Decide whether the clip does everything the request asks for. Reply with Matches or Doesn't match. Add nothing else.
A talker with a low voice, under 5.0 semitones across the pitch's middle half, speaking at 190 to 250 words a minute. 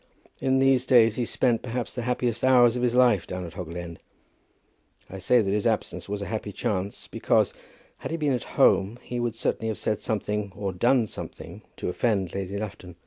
Matches